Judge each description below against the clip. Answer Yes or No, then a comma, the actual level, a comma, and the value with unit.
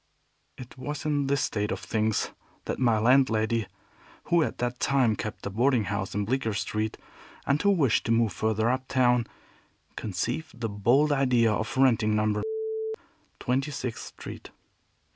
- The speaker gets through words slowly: No, average, 155 wpm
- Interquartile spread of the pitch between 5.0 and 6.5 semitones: No, average, 3.7 semitones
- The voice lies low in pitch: Yes, low, 120 Hz